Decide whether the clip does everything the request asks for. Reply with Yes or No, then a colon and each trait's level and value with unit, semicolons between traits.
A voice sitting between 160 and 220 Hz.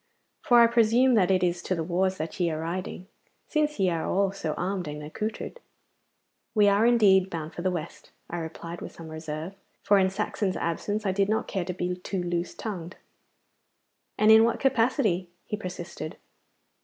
Yes: medium, 185 Hz